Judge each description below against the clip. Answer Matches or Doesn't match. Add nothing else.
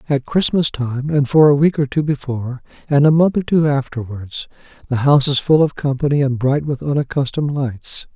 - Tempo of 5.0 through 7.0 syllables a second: Matches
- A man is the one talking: Matches